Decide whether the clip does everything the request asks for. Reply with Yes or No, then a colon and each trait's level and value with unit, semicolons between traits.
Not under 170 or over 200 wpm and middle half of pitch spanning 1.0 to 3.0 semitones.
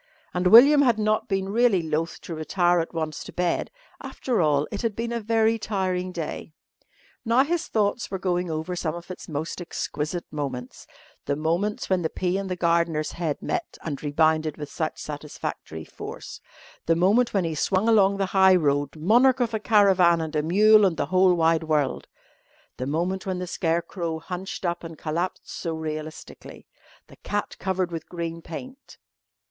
No: average, 180 wpm; average, 4.0 semitones